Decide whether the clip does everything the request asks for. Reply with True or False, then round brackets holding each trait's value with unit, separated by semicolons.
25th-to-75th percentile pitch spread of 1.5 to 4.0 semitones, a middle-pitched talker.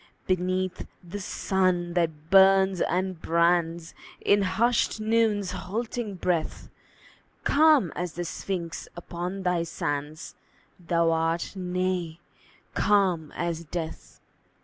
True (2.4 semitones; 180 Hz)